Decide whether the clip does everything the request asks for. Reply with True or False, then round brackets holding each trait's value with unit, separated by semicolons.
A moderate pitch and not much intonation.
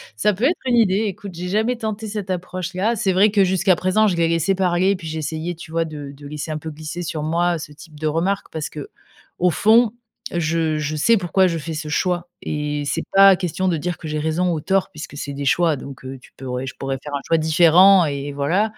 False (170 Hz; 3.9 semitones)